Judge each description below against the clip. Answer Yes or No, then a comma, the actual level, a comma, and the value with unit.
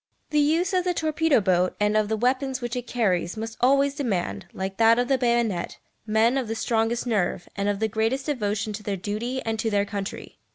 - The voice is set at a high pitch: Yes, high, 225 Hz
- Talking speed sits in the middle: No, fast, 215 wpm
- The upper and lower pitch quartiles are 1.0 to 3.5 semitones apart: No, average, 3.9 semitones